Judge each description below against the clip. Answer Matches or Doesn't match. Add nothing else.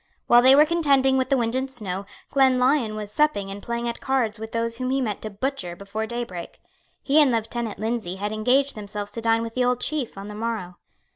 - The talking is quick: Matches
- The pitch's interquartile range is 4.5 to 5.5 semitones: Doesn't match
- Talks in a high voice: Matches